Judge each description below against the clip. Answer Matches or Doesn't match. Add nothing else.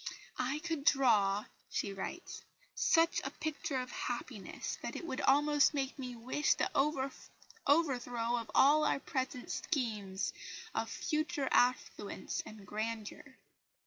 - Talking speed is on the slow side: Matches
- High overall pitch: Matches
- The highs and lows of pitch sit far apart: Doesn't match